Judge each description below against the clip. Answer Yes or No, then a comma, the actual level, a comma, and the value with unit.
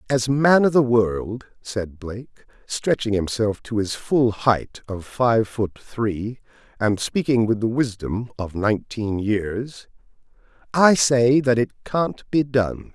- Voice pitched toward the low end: Yes, low, 115 Hz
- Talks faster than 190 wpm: No, average, 150 wpm